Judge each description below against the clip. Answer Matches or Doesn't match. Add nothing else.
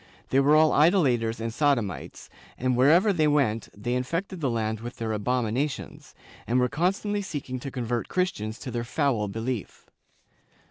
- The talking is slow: Doesn't match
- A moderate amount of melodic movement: Matches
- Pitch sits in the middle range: Doesn't match